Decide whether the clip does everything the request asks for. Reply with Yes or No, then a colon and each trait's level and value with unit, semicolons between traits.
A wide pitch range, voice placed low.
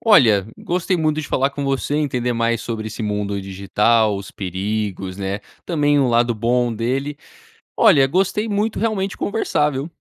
Yes: wide, 6.1 semitones; low, 125 Hz